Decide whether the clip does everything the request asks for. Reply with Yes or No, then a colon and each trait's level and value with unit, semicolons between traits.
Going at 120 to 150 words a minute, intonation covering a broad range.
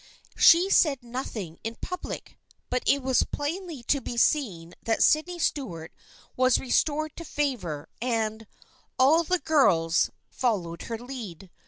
Yes: average, 145 wpm; wide, 5.7 semitones